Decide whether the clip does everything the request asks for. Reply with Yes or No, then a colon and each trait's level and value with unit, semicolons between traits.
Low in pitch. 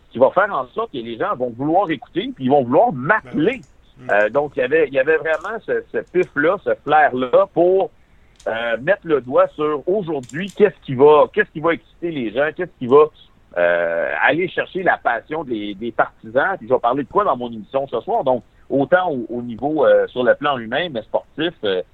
No: medium, 155 Hz